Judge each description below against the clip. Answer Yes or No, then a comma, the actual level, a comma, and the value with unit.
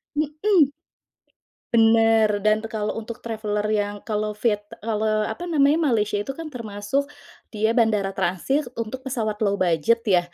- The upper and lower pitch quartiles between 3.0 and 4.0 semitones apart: Yes, average, 3.5 semitones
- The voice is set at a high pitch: Yes, high, 220 Hz